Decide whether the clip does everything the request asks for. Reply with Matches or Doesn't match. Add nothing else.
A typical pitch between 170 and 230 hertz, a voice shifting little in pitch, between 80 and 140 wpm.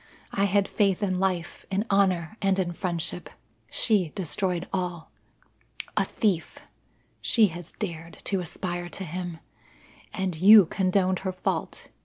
Matches